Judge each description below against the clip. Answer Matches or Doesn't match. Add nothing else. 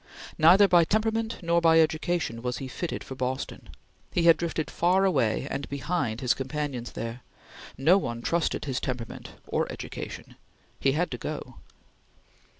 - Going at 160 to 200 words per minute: Doesn't match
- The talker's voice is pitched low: Doesn't match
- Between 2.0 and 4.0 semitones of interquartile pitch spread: Doesn't match